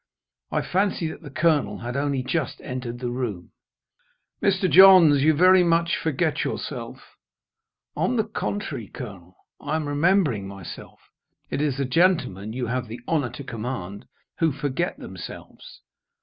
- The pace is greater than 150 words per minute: No, average, 145 wpm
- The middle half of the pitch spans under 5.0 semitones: No, wide, 5.6 semitones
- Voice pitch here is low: No, medium, 145 Hz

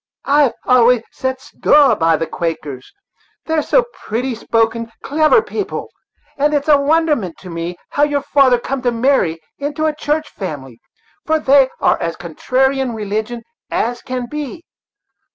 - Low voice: No, very high, 255 Hz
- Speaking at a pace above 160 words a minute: No, average, 155 wpm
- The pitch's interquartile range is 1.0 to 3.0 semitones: No, average, 5.1 semitones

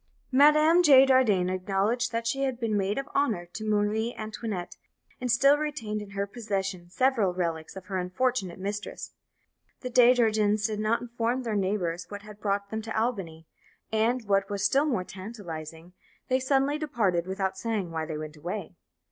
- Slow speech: No, average, 175 wpm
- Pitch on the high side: Yes, high, 210 Hz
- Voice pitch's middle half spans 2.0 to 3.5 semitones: No, average, 4.4 semitones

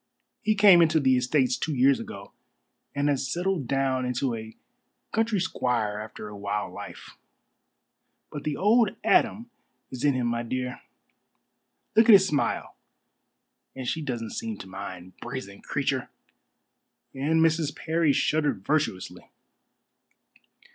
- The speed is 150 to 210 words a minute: No, slow, 135 wpm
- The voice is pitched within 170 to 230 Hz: No, low, 135 Hz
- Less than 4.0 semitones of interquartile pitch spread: No, wide, 5.4 semitones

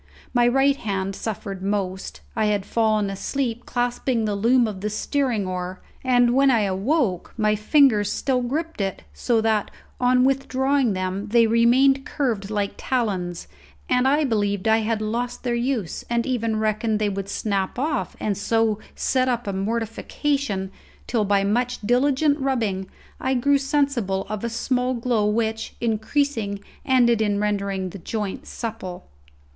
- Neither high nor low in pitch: No, high, 225 Hz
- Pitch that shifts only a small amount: No, average, 3.8 semitones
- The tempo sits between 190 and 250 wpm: No, average, 155 wpm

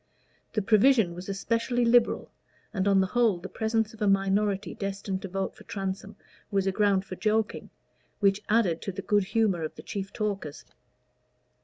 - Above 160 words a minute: Yes, average, 175 wpm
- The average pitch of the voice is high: Yes, high, 200 Hz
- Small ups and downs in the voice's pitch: Yes, narrow, 2.2 semitones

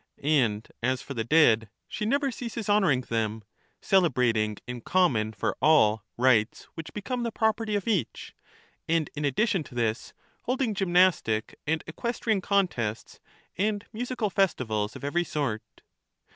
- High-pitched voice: No, medium, 155 Hz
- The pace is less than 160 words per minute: Yes, average, 140 wpm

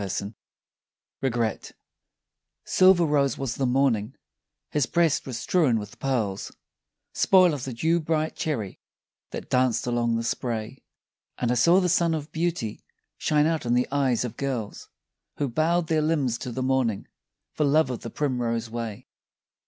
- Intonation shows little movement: No, average, 4.9 semitones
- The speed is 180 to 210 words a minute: No, average, 155 wpm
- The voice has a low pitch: Yes, low, 130 Hz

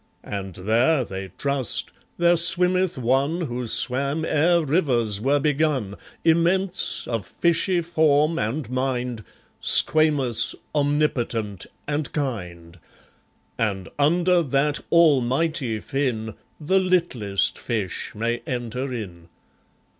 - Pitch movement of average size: No, wide, 5.9 semitones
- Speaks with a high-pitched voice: No, low, 135 Hz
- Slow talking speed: Yes, slow, 100 wpm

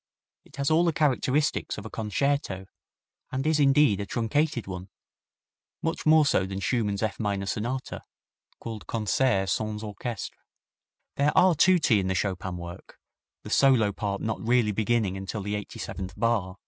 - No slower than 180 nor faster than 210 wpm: No, average, 160 wpm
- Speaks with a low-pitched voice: Yes, low, 110 Hz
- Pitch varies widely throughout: Yes, wide, 5.7 semitones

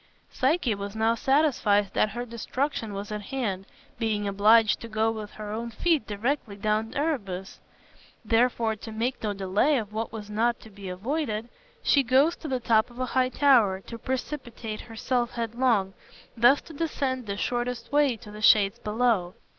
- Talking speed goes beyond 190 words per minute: No, average, 175 wpm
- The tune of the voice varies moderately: Yes, average, 3.4 semitones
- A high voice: Yes, high, 225 Hz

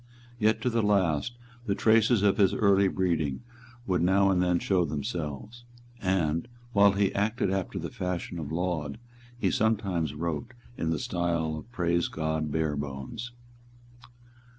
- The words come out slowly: No, average, 145 wpm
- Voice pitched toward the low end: Yes, very low, 90 Hz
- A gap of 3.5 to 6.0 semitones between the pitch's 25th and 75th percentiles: Yes, average, 4.1 semitones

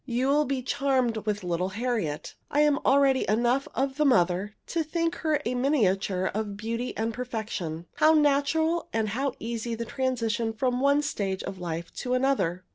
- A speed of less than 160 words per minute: No, average, 175 wpm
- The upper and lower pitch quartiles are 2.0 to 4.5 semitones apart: No, average, 4.9 semitones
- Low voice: No, high, 240 Hz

